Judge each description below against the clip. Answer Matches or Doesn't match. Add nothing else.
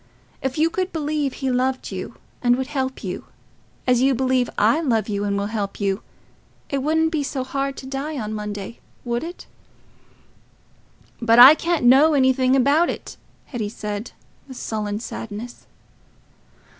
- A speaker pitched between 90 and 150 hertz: Doesn't match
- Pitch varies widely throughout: Doesn't match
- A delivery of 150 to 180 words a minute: Matches